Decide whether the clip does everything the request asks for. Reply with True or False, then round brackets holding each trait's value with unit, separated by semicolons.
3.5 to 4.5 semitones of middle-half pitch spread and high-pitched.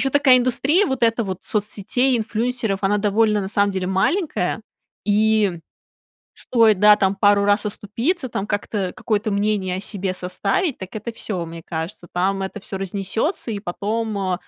False (2.9 semitones; 205 Hz)